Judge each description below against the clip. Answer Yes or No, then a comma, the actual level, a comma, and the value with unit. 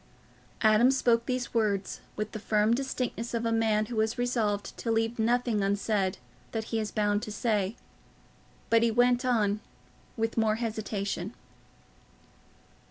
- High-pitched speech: Yes, high, 225 Hz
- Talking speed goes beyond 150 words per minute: No, average, 145 wpm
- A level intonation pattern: Yes, narrow, 2.0 semitones